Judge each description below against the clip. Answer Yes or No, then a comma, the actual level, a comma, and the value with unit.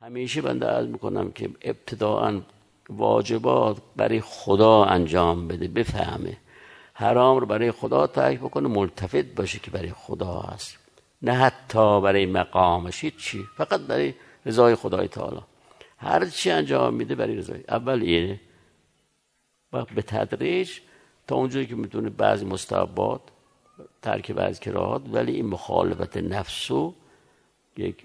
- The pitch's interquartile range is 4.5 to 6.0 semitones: Yes, average, 5.1 semitones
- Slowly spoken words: No, average, 125 wpm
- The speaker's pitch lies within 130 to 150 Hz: No, low, 105 Hz